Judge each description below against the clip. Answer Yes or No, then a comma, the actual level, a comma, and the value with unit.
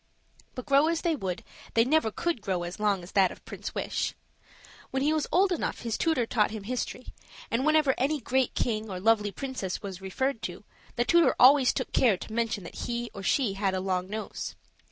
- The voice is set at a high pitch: Yes, high, 230 Hz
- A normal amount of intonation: No, wide, 5.7 semitones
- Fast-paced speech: Yes, fast, 210 wpm